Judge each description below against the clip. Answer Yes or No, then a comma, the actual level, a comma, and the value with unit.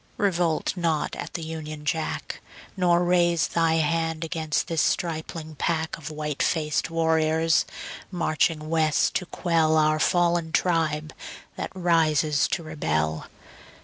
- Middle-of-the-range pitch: Yes, medium, 160 Hz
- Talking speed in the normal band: No, slow, 125 wpm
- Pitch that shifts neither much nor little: No, narrow, 1.5 semitones